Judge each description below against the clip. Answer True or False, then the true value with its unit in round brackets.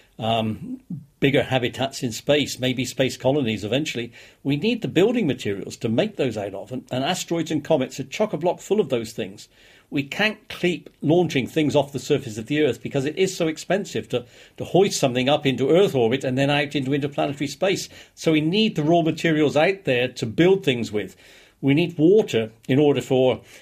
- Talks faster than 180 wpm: True (205 wpm)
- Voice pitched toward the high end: False (140 Hz)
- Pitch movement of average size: True (4.6 semitones)